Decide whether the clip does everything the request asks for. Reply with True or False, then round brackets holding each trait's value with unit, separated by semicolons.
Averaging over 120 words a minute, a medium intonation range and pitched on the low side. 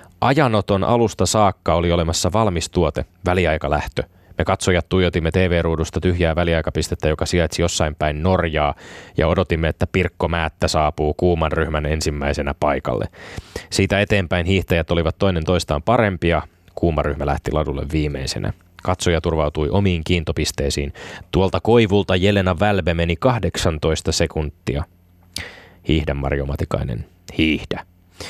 False (115 wpm; 3.1 semitones; 85 Hz)